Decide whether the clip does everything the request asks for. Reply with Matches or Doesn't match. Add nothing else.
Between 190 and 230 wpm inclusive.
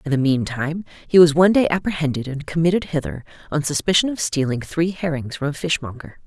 Matches